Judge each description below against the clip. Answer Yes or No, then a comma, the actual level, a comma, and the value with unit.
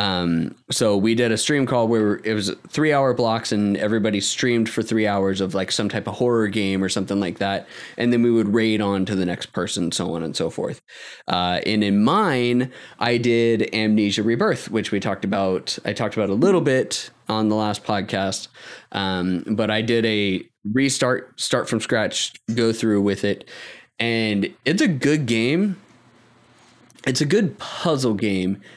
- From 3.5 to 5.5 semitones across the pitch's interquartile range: No, average, 2.9 semitones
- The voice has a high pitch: No, low, 110 Hz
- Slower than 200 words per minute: Yes, average, 190 wpm